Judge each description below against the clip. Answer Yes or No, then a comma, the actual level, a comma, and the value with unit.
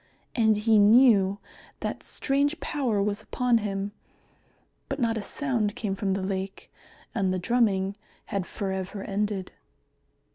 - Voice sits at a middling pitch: No, high, 210 Hz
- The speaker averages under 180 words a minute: Yes, average, 140 wpm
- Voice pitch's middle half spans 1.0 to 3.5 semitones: Yes, average, 3.1 semitones